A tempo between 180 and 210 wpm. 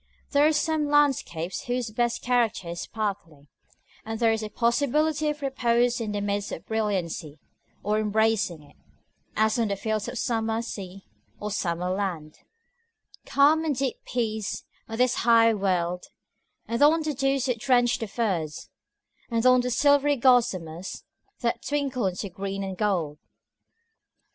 No: average, 150 wpm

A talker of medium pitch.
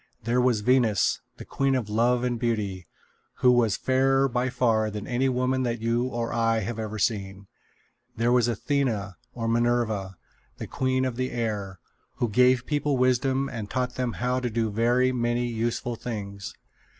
No: low, 120 Hz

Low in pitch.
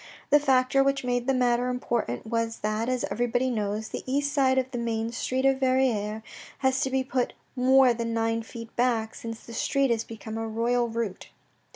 No: high, 240 Hz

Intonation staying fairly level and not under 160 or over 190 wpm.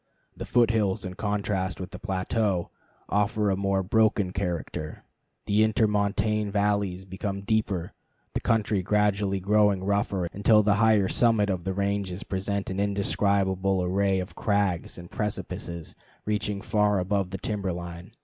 No: narrow, 1.8 semitones; average, 145 wpm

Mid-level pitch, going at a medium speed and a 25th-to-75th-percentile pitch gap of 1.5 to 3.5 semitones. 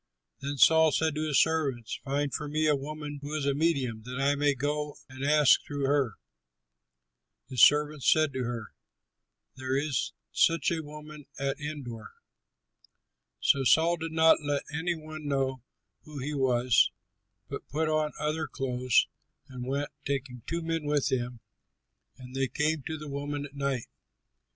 Yes: medium, 145 Hz; average, 160 wpm; narrow, 2.4 semitones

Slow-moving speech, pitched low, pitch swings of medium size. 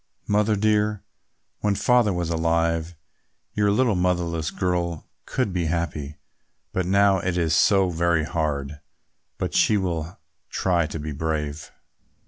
Yes: slow, 130 wpm; very low, 85 Hz; average, 3.6 semitones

